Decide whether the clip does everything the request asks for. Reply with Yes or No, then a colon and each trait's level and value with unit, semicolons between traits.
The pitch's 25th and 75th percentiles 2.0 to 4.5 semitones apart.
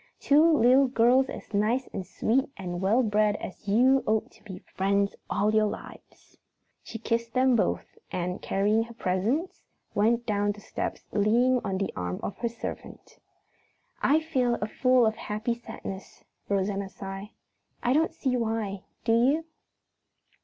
Yes: average, 3.8 semitones